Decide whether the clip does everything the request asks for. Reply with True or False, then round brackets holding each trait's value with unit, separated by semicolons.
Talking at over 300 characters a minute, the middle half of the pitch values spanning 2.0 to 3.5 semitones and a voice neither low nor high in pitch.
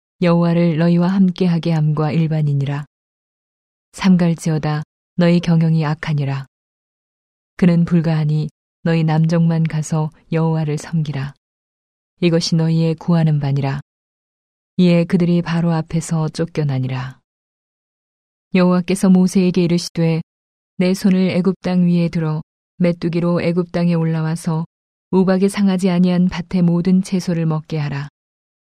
False (280 characters per minute; 2.4 semitones; 165 Hz)